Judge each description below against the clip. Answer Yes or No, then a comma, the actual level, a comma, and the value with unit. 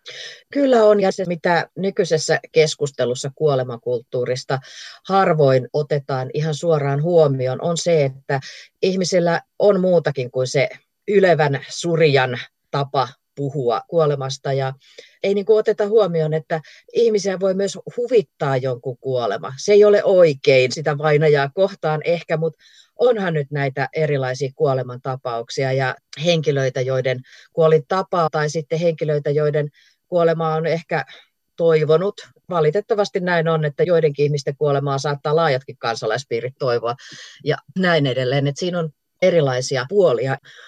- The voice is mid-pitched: Yes, medium, 155 Hz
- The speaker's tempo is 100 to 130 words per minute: Yes, average, 125 wpm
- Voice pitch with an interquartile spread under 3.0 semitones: No, average, 4.2 semitones